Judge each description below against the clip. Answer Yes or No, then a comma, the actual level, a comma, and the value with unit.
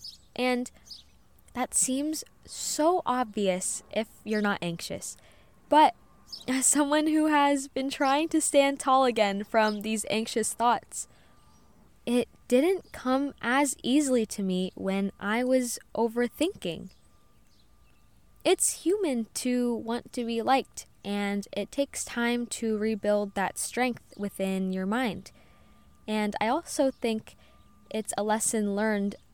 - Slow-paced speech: Yes, slow, 125 wpm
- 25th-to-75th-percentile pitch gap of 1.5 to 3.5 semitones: No, average, 4.5 semitones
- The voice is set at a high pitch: Yes, high, 240 Hz